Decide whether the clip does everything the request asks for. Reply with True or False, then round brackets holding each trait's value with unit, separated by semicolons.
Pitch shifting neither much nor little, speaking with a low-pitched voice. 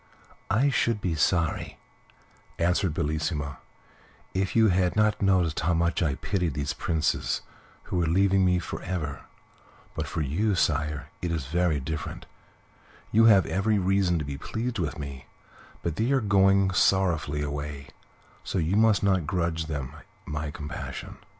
True (4.3 semitones; 85 Hz)